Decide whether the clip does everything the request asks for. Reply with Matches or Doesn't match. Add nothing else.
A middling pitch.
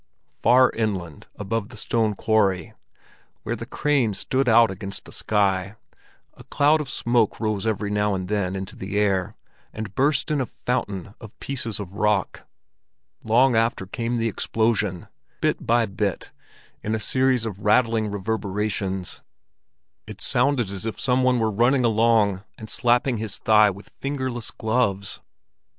Doesn't match